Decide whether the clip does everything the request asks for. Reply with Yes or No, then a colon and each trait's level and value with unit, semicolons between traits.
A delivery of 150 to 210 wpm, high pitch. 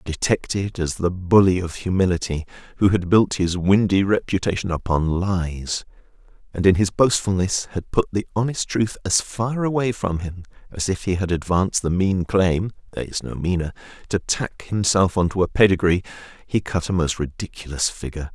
No: average, 175 wpm; very low, 95 Hz